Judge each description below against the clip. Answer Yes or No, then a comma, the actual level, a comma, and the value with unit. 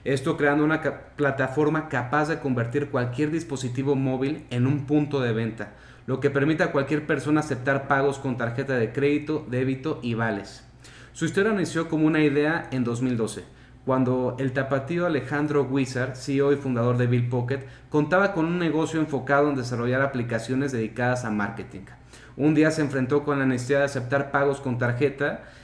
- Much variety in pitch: No, average, 2.7 semitones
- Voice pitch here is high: No, medium, 140 Hz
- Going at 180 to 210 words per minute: No, average, 170 wpm